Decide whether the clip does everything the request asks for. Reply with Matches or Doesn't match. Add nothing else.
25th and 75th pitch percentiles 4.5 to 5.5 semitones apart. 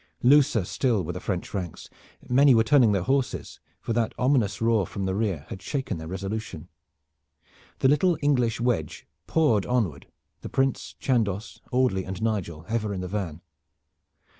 Matches